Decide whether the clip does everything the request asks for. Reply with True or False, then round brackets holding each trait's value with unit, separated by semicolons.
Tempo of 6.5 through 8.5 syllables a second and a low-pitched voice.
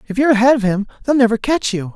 False (7.5 syllables/s; 230 Hz)